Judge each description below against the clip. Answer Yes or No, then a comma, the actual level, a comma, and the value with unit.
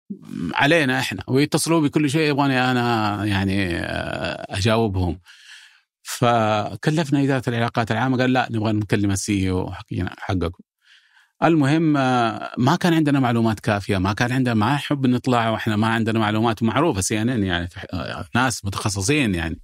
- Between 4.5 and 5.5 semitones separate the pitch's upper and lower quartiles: Yes, average, 4.8 semitones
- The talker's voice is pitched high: No, low, 115 Hz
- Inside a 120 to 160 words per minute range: Yes, fast, 135 wpm